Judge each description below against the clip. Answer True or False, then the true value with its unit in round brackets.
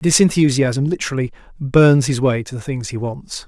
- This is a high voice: False (135 Hz)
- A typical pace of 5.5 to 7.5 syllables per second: False (5.1 syllables/s)